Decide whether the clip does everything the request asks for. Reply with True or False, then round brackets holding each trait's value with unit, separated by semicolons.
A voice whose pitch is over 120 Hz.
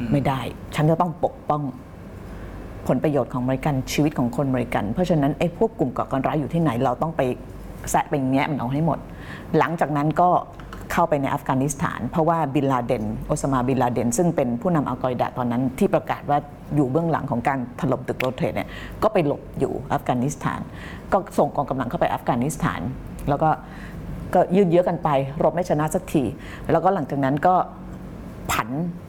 True (140 Hz)